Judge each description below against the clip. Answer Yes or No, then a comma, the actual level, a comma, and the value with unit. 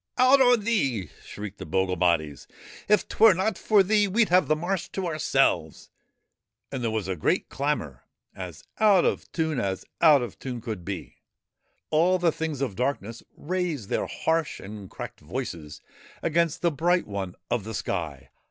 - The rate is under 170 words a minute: No, average, 180 wpm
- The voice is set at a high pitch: No, low, 135 Hz